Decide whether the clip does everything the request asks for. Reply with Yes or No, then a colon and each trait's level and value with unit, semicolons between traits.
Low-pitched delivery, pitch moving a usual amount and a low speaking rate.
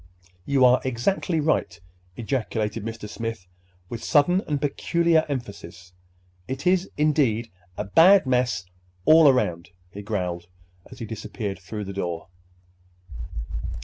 No: low, 115 Hz; wide, 6.4 semitones; slow, 120 wpm